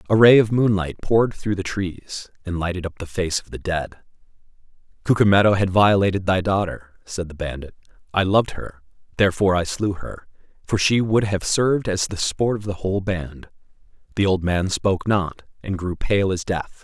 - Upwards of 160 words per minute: Yes, average, 185 wpm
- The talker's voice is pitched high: No, very low, 95 Hz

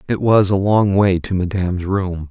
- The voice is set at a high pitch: No, very low, 95 Hz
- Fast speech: Yes, fast, 210 wpm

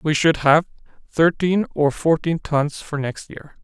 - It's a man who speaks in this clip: Yes, male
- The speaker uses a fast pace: No, average, 165 wpm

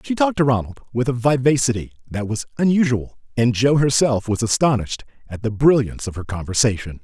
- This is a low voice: Yes, low, 120 Hz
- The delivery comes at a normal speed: Yes, average, 180 wpm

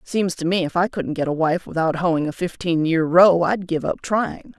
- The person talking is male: No, female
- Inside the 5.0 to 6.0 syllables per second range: No, 4.7 syllables/s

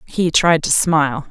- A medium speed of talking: Yes, average, 185 wpm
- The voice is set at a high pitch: No, medium, 155 Hz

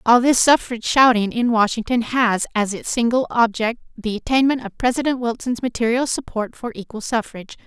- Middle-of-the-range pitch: No, high, 235 Hz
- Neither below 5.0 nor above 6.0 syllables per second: Yes, 5.5 syllables/s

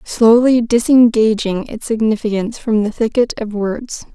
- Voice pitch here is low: No, high, 225 Hz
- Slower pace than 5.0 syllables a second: Yes, 4.6 syllables/s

